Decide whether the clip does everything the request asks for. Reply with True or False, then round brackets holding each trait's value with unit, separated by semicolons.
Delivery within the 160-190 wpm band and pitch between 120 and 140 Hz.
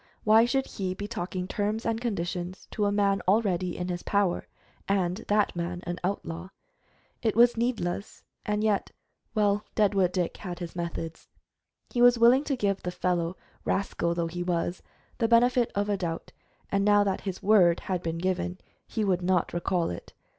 False (175 wpm; 190 Hz)